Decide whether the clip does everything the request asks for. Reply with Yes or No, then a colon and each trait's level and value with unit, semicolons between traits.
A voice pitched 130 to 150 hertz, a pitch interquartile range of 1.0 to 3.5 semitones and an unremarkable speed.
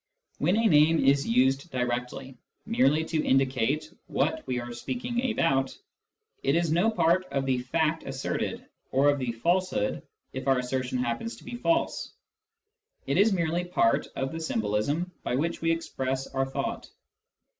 No: medium, 140 Hz; average, 4.8 semitones; average, 155 wpm